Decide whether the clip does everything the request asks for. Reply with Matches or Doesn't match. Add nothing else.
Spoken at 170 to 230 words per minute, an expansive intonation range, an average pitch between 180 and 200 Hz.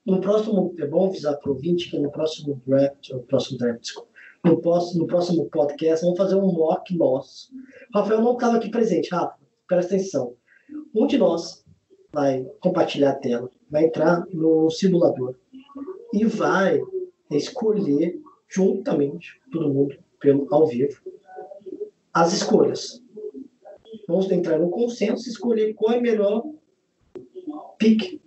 Doesn't match